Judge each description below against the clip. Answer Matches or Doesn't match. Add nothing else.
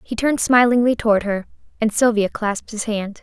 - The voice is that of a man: Doesn't match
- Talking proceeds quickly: Doesn't match